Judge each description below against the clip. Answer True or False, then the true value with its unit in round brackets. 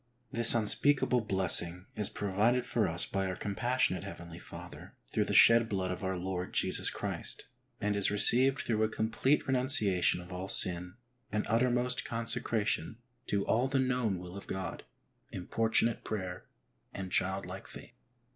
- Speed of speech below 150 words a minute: False (155 wpm)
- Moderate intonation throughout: True (4.1 semitones)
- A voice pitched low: True (105 Hz)